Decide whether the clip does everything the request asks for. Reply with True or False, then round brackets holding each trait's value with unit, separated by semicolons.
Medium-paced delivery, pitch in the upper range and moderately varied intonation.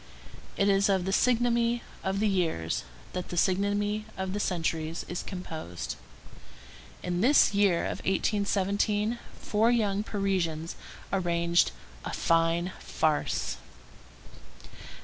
False (110 wpm; 195 Hz; 3.2 semitones)